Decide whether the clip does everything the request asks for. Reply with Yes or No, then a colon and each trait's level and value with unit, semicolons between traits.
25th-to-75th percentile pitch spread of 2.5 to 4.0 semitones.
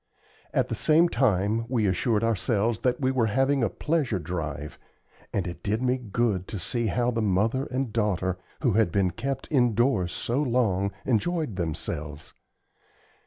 No: average, 5.0 semitones